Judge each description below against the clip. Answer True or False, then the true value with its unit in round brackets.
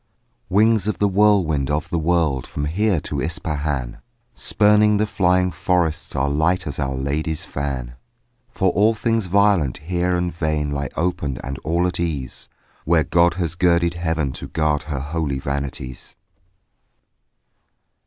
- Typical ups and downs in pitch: True (4.0 semitones)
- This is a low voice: True (80 Hz)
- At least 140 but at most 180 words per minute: True (145 wpm)